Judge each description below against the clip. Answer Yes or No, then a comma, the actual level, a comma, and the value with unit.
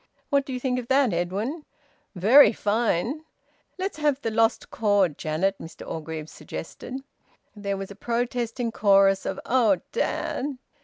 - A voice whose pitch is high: Yes, high, 225 Hz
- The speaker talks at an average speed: Yes, average, 145 wpm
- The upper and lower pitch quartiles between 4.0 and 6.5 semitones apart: Yes, average, 4.9 semitones